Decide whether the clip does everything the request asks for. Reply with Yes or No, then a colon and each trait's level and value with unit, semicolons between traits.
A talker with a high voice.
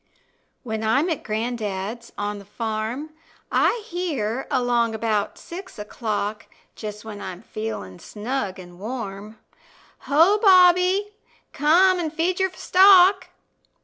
Yes: high, 235 Hz